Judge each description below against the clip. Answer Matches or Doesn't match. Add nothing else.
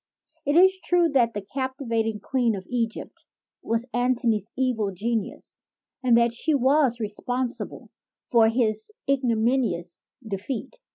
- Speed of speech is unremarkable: Doesn't match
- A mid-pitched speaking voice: Doesn't match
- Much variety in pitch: Doesn't match